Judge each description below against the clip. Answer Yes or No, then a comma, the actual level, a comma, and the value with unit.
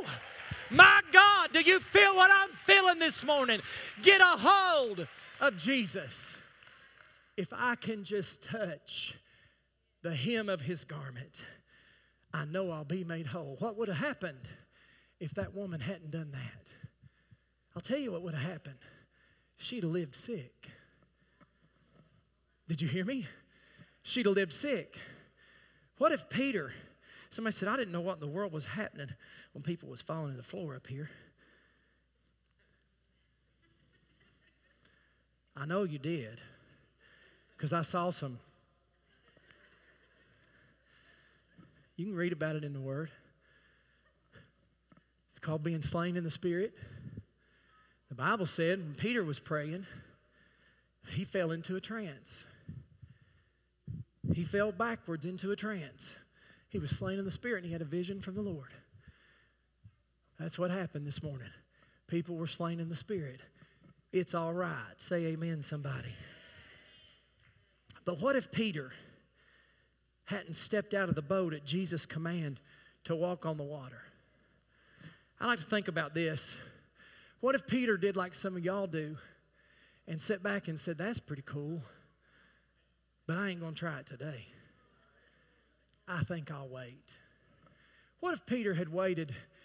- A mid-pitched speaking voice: Yes, medium, 170 Hz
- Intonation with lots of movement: Yes, wide, 5.7 semitones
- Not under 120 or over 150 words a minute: Yes, average, 145 wpm